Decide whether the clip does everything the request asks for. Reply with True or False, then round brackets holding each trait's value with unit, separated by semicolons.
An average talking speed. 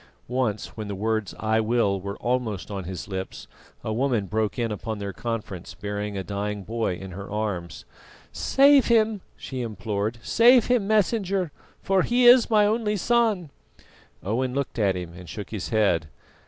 True (170 wpm)